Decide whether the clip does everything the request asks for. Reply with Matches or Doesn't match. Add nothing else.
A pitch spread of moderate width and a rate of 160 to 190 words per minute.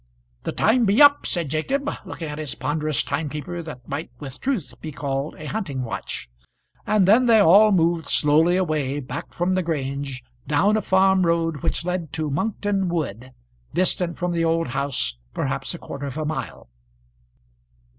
Matches